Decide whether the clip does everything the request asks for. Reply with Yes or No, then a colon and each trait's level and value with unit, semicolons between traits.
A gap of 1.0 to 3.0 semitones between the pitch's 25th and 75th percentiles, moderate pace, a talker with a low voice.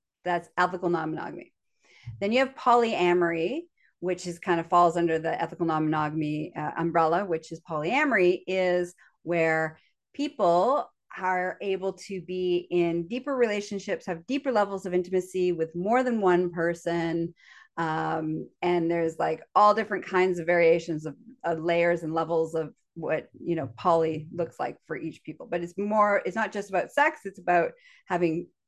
No: average, 2.7 semitones; average, 165 wpm; medium, 175 Hz